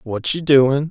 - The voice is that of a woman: No, male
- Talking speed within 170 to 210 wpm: Yes, average, 200 wpm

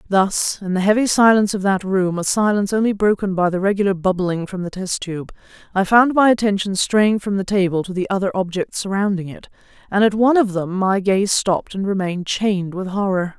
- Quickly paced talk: Yes, fast, 210 wpm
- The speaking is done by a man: No, female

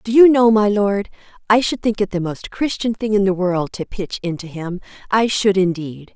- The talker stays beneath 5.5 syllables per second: Yes, 4.9 syllables/s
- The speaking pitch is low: No, high, 200 Hz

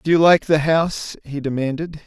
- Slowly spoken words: No, fast, 205 wpm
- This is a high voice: No, medium, 155 Hz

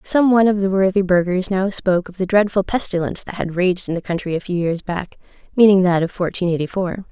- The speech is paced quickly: Yes, fast, 235 wpm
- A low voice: No, medium, 185 Hz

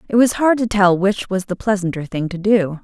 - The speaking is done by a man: No, female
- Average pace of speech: No, fast, 255 wpm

